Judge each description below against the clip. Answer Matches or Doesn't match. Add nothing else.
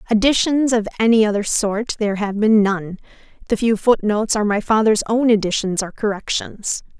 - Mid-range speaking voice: Doesn't match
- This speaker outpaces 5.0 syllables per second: Matches